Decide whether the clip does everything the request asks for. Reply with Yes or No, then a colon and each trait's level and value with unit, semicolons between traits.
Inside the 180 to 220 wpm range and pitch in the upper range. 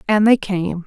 Yes: fast, 210 wpm; high, 195 Hz